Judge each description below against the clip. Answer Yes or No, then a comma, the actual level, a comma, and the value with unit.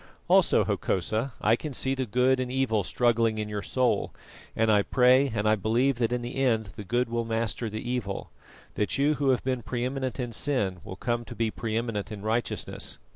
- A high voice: No, low, 120 Hz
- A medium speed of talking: No, fast, 210 wpm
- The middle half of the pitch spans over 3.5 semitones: No, average, 2.8 semitones